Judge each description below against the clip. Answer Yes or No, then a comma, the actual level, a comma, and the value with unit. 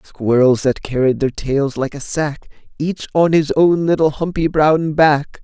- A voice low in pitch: No, medium, 150 Hz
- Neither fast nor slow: Yes, average, 175 wpm